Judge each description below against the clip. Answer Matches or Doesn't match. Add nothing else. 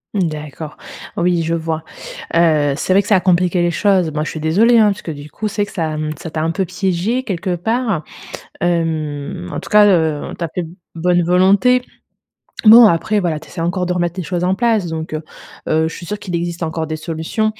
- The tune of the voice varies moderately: Matches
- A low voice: Doesn't match